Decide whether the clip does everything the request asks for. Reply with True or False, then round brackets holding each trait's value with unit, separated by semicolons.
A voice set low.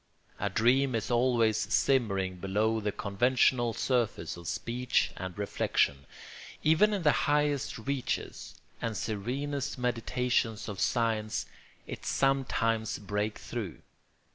True (115 Hz)